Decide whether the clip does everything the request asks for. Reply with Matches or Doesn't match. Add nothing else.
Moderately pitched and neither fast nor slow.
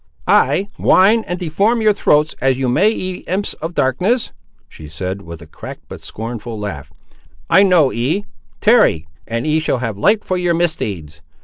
Matches